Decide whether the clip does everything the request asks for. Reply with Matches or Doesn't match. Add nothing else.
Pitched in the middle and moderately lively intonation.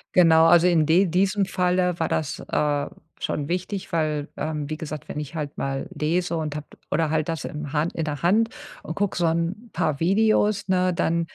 Matches